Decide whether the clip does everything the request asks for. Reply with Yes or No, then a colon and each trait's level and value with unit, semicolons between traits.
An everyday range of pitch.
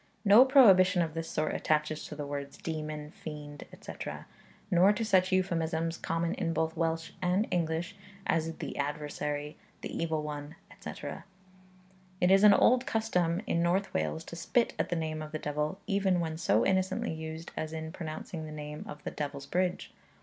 Yes: average, 3.1 semitones